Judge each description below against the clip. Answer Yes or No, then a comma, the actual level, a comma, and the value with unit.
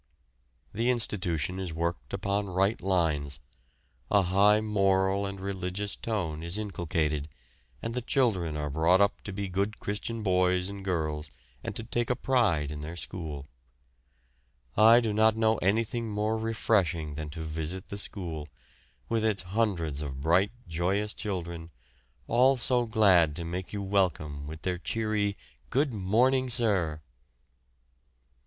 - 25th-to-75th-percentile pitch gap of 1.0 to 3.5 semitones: No, average, 4.6 semitones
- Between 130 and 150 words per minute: Yes, average, 145 wpm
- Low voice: Yes, very low, 95 Hz